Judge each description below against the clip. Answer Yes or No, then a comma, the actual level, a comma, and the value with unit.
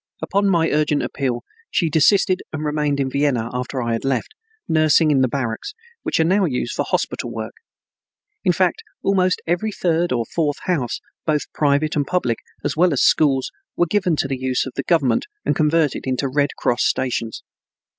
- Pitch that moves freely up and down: No, average, 4.3 semitones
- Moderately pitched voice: Yes, medium, 150 Hz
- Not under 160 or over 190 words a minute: Yes, average, 185 wpm